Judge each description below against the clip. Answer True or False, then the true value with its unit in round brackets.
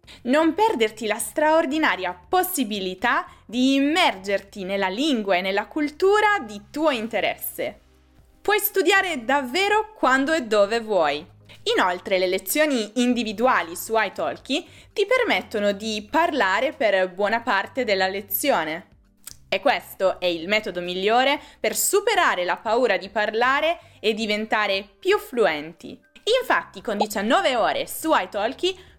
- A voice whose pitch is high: True (245 Hz)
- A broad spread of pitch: True (8.0 semitones)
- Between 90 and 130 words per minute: True (120 wpm)